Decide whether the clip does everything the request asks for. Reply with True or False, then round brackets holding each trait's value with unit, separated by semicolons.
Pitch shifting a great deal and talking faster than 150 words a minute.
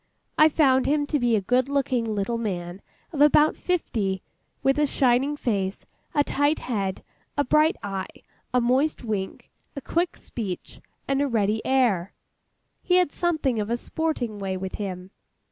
True (6.2 semitones; 160 wpm)